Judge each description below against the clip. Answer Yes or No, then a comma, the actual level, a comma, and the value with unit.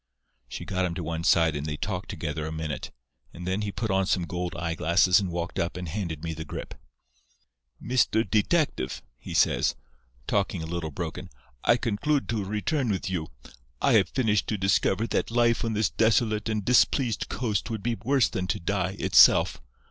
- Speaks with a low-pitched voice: Yes, very low, 95 Hz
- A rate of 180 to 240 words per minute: Yes, average, 185 wpm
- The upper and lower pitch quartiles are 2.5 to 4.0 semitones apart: No, average, 4.7 semitones